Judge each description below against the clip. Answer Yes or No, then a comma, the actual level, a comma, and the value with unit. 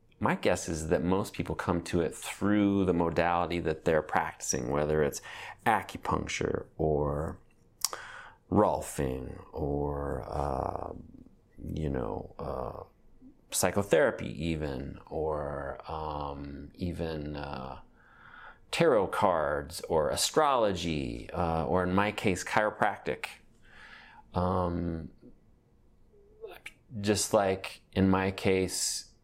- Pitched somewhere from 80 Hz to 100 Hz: Yes, very low, 85 Hz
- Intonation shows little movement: No, average, 4.3 semitones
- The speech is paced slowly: Yes, slow, 95 wpm